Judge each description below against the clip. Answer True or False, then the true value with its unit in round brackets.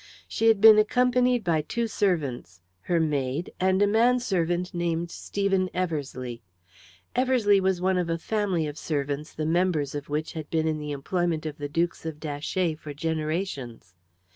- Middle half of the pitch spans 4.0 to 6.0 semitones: True (4.3 semitones)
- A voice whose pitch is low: False (170 Hz)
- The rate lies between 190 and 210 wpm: False (165 wpm)